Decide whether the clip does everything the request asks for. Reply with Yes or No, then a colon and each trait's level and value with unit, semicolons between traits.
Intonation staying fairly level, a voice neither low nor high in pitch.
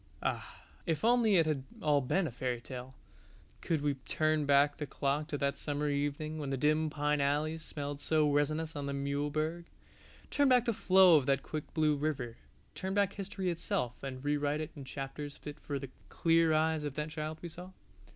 Yes: narrow, 2.2 semitones; medium, 150 Hz